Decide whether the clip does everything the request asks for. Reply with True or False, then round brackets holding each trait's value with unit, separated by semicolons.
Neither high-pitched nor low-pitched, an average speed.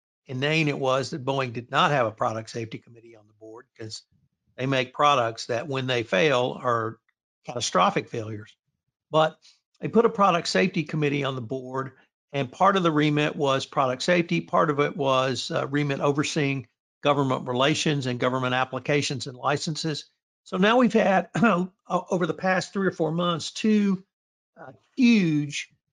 True (145 Hz; 170 wpm)